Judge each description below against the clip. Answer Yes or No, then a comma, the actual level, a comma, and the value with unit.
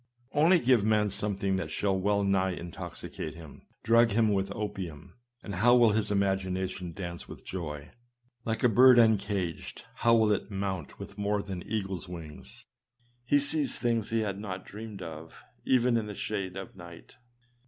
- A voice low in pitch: Yes, low, 100 Hz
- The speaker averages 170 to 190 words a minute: Yes, average, 175 wpm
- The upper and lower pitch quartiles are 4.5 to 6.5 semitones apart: No, average, 3.2 semitones